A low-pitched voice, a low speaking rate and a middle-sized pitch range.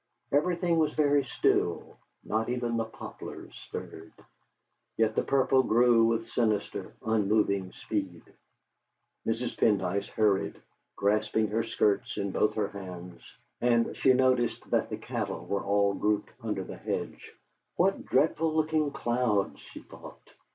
Yes: low, 110 Hz; slow, 130 wpm; average, 3.8 semitones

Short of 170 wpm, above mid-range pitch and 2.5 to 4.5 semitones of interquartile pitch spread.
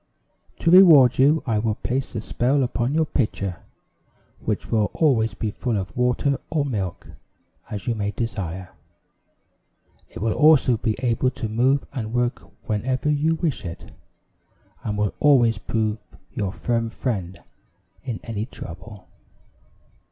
No: average, 140 wpm; low, 115 Hz; average, 4.1 semitones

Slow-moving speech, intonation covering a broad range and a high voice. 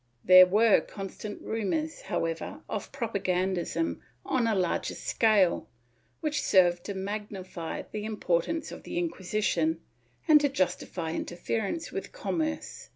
No: slow, 125 wpm; average, 4.4 semitones; high, 200 Hz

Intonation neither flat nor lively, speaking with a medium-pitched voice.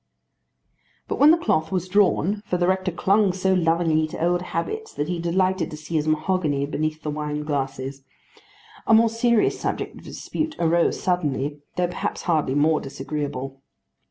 Yes: average, 3.9 semitones; medium, 170 Hz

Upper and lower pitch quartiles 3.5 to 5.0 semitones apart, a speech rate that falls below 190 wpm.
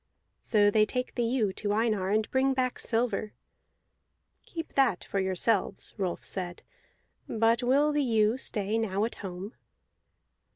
Yes: average, 3.8 semitones; average, 140 wpm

